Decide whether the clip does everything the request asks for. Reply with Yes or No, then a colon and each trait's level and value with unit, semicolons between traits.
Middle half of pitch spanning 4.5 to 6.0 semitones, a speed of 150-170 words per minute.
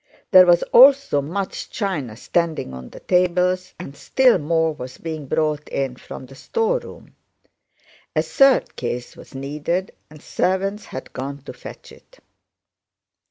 No: average, 5.3 semitones; average, 140 wpm